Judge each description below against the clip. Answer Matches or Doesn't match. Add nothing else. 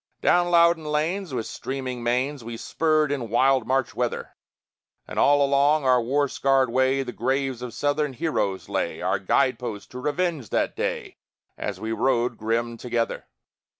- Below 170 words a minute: Matches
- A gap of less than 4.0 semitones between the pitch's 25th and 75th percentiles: Matches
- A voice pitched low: Matches